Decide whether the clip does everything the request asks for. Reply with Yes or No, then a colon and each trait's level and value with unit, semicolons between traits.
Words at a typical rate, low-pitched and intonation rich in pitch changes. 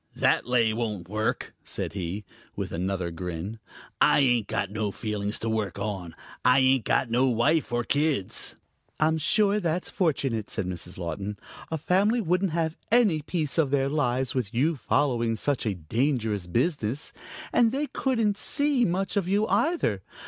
Yes: average, 165 wpm; low, 125 Hz; wide, 7.6 semitones